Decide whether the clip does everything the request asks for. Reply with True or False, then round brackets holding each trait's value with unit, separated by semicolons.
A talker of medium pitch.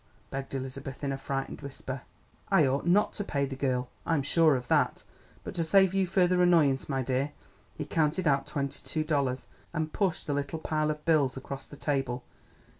True (145 Hz)